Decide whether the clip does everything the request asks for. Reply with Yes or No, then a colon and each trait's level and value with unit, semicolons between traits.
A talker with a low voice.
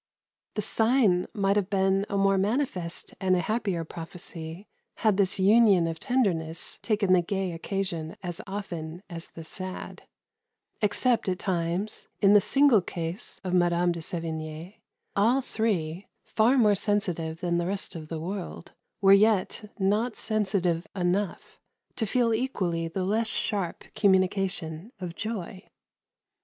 No: high, 190 Hz